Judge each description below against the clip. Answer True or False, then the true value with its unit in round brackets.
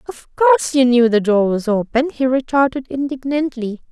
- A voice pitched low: False (260 Hz)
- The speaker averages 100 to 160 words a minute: False (170 wpm)